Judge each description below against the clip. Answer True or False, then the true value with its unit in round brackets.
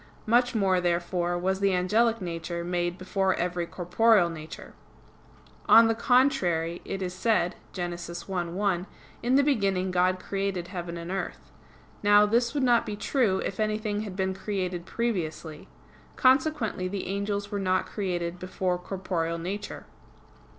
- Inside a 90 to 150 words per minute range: True (145 wpm)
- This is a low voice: False (190 Hz)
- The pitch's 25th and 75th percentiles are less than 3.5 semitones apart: True (3.1 semitones)